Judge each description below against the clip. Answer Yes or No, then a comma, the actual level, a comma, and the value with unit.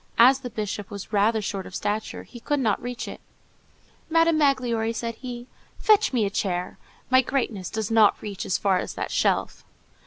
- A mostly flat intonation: No, average, 3.9 semitones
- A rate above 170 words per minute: Yes, average, 190 wpm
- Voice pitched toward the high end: Yes, high, 225 Hz